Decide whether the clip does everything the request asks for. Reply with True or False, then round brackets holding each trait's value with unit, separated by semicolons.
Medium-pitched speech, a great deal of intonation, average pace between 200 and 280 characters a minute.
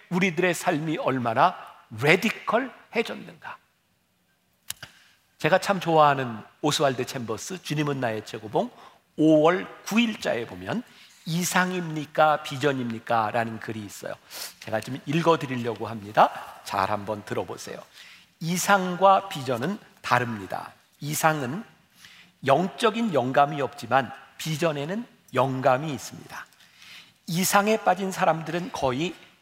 True (155 Hz; 6.2 semitones; 255 characters per minute)